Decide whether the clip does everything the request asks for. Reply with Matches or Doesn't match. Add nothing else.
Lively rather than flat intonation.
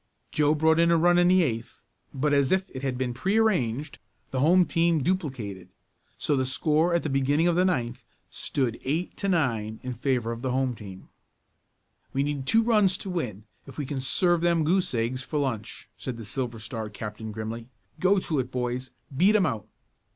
Matches